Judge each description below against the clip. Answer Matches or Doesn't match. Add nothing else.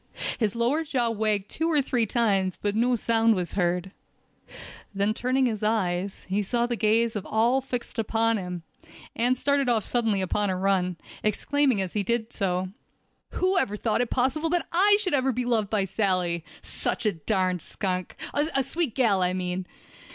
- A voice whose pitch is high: Matches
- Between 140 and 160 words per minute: Doesn't match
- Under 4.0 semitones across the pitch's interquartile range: Doesn't match